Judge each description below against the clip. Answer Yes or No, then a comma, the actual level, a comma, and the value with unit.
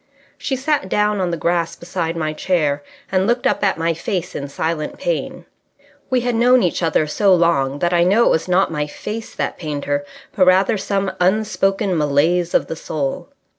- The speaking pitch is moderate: Yes, medium, 180 Hz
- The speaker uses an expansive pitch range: No, average, 3.9 semitones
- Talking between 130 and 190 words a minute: No, average, 200 wpm